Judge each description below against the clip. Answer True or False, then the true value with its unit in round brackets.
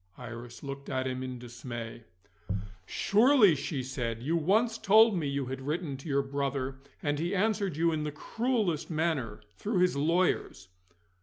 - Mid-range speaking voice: True (145 Hz)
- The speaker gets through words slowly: False (160 wpm)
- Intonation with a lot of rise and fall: True (5.8 semitones)